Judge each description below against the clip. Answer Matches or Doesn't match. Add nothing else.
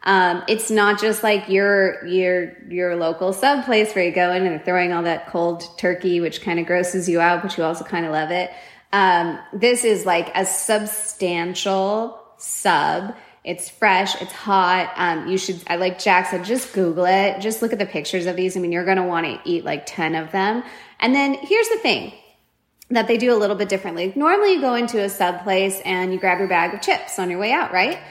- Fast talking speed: Matches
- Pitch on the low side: Doesn't match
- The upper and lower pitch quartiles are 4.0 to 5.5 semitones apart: Doesn't match